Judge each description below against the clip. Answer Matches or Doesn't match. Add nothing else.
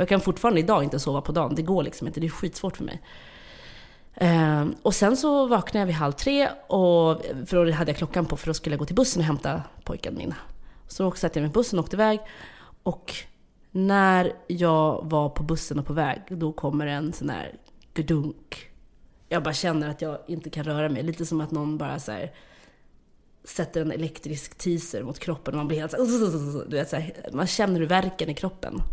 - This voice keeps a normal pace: Doesn't match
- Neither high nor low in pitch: Matches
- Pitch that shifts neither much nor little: Matches